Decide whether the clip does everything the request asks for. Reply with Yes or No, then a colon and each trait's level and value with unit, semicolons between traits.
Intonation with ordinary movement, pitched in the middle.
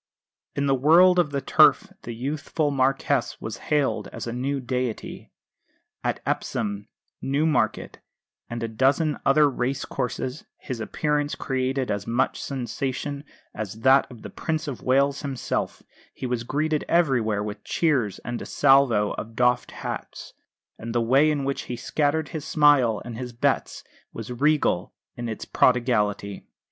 No: average, 3.6 semitones; low, 130 Hz